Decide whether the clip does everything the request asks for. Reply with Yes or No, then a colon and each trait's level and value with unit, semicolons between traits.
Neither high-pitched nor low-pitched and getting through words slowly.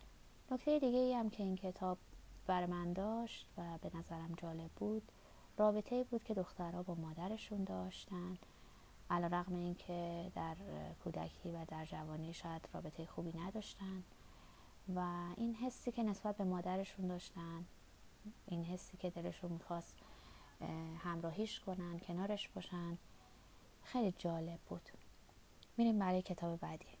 No: medium, 180 Hz; average, 130 wpm